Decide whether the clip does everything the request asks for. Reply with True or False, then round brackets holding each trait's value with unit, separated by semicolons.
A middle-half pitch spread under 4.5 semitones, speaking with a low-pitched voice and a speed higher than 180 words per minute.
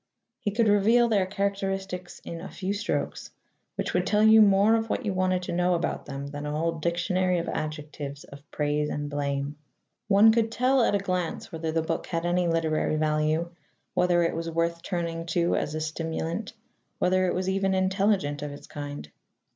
False (4.0 semitones; 175 Hz; 190 wpm)